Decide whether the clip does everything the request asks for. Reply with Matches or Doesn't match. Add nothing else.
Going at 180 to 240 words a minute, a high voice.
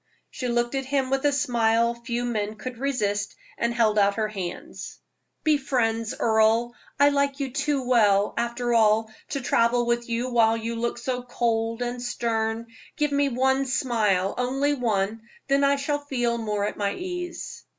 Doesn't match